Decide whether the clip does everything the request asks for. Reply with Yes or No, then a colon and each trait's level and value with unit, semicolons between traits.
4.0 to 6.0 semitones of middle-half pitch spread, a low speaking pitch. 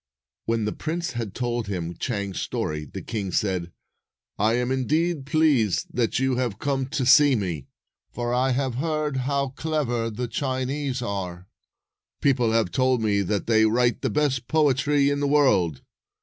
Yes: average, 4.6 semitones; low, 125 Hz